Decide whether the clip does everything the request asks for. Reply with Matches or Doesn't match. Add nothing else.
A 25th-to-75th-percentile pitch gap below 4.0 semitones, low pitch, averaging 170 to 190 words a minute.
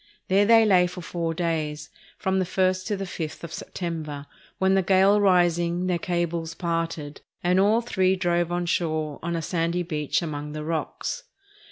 Doesn't match